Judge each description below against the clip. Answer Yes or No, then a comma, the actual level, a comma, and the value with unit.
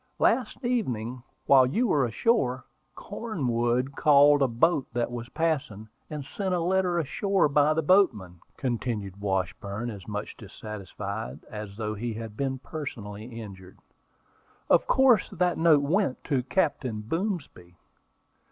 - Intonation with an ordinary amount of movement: No, wide, 7.4 semitones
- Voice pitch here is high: No, low, 130 Hz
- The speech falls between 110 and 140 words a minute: Yes, slow, 135 wpm